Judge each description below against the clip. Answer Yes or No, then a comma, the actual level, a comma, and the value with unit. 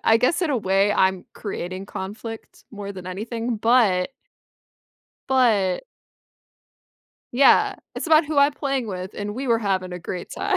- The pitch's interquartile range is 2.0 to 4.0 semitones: No, average, 5.2 semitones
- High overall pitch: Yes, high, 215 Hz